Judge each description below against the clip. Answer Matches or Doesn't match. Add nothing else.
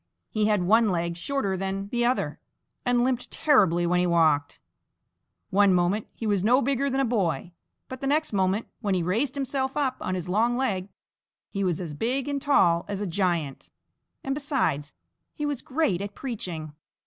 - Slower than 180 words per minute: Doesn't match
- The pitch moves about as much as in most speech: Doesn't match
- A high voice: Matches